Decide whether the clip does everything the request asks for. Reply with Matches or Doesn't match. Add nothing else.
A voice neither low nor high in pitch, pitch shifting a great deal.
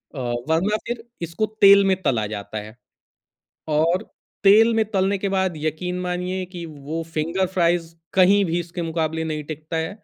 Doesn't match